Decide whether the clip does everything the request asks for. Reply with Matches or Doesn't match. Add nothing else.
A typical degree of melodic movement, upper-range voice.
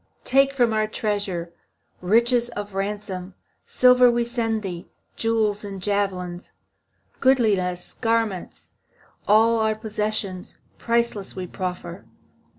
Matches